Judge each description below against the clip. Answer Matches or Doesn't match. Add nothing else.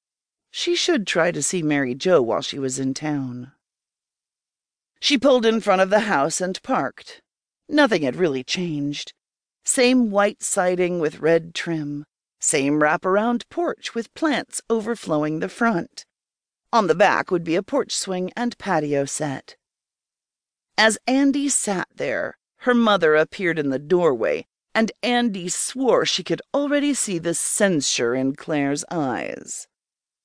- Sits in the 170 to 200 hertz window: Matches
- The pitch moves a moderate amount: Doesn't match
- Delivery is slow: Doesn't match